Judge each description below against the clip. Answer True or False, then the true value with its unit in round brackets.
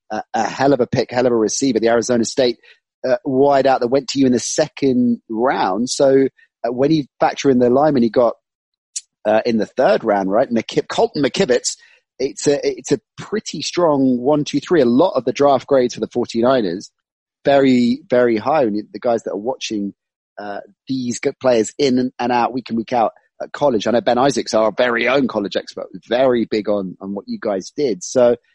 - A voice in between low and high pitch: False (125 Hz)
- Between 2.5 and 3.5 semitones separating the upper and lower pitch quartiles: True (2.8 semitones)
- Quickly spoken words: True (220 wpm)